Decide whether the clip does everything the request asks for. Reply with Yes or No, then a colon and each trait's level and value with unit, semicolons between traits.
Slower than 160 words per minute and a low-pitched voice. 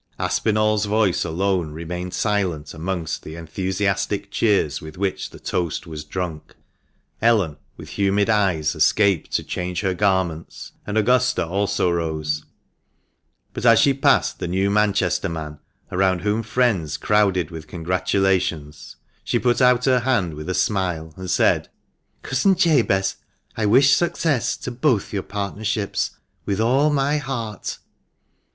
Yes: average, 140 wpm; very low, 95 Hz